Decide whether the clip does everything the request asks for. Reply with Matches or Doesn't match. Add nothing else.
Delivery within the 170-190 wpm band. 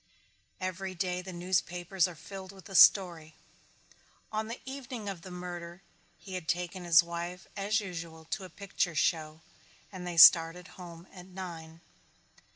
Doesn't match